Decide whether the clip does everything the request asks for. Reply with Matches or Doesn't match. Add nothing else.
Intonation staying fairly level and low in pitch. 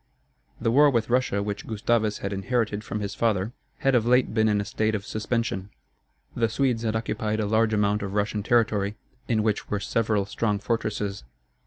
Matches